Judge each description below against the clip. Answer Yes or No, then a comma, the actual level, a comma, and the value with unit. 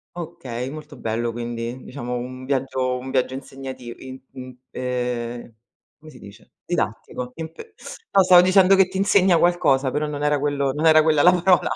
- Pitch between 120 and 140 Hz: Yes, low, 135 Hz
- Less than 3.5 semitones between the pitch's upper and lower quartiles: No, average, 4.3 semitones